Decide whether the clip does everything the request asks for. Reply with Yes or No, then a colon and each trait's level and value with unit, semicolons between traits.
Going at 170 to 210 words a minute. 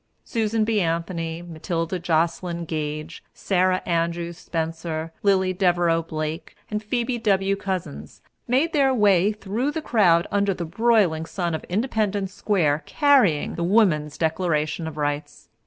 No: slow, 135 wpm